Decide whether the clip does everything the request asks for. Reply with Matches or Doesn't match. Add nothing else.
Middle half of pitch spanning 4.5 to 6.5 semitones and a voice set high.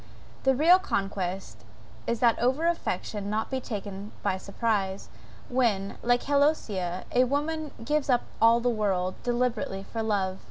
Matches